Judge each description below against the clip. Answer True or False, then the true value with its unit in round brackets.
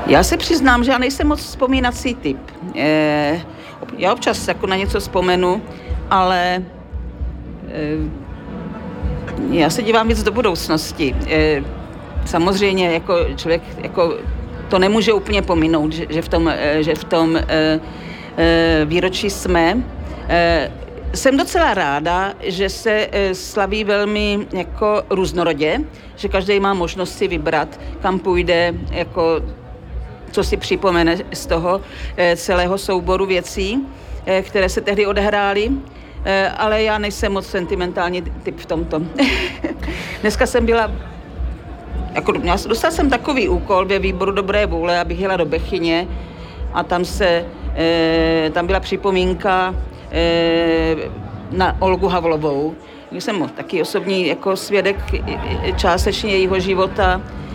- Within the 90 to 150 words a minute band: True (120 wpm)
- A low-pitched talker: False (185 Hz)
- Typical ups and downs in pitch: True (3.5 semitones)